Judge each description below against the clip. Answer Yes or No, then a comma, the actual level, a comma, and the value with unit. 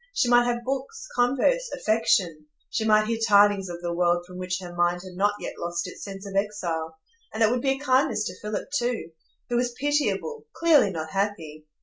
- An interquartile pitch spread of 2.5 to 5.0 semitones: No, wide, 5.5 semitones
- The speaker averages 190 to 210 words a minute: Yes, average, 200 wpm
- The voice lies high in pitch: Yes, high, 205 Hz